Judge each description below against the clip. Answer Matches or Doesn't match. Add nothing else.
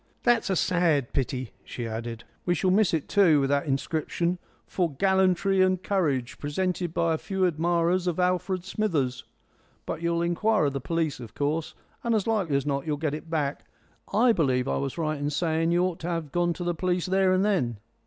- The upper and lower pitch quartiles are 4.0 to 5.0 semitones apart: Matches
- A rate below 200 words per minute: Doesn't match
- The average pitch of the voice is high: Doesn't match